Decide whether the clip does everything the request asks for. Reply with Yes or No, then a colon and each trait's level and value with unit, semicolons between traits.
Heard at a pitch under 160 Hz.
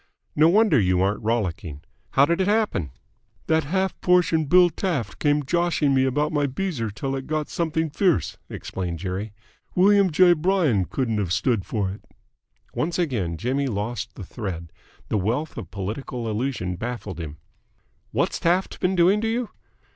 Yes: low, 135 Hz